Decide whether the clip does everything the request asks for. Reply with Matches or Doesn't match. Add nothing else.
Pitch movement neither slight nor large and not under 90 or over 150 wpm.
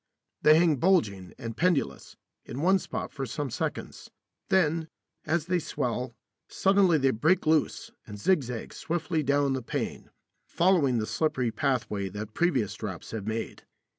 Doesn't match